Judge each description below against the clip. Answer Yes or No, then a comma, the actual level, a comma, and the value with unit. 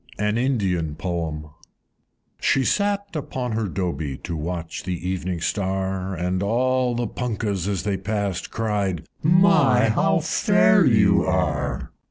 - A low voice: Yes, low, 100 Hz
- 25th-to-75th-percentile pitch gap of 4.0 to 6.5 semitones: Yes, average, 5.3 semitones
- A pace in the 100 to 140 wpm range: Yes, slow, 135 wpm